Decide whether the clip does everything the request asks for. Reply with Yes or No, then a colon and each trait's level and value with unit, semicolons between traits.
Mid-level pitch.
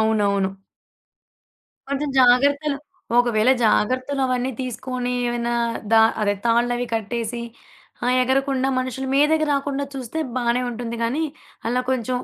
No: very high, 250 Hz